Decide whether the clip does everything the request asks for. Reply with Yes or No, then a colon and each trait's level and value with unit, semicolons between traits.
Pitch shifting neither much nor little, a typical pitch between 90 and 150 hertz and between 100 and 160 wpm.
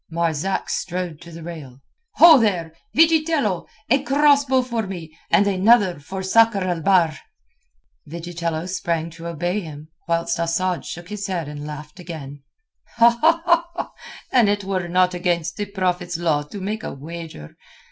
No: average, 4.0 semitones; medium, 180 Hz; average, 145 wpm